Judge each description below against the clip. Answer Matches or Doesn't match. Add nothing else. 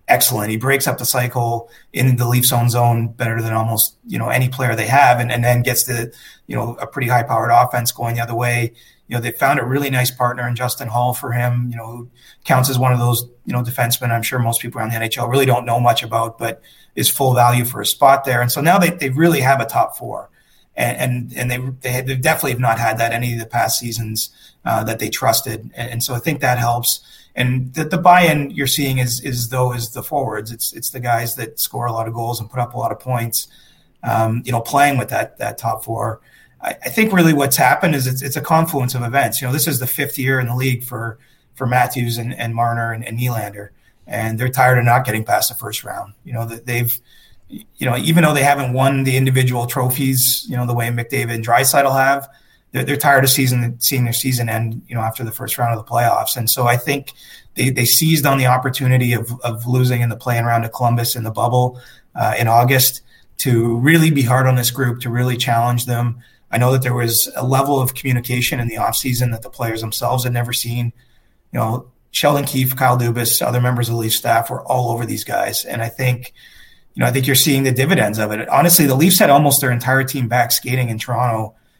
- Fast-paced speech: Matches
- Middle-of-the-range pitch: Doesn't match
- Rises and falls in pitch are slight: Matches